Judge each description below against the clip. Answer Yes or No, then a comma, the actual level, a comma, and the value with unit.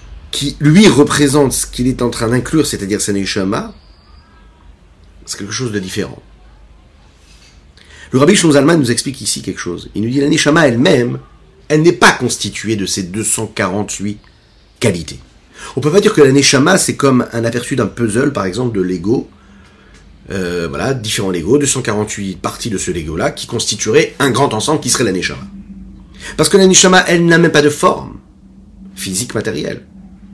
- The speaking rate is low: No, average, 175 wpm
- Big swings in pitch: Yes, wide, 7.4 semitones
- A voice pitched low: Yes, low, 110 Hz